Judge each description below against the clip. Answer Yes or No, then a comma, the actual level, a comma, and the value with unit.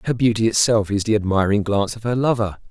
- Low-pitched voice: Yes, low, 110 Hz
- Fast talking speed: Yes, fast, 220 wpm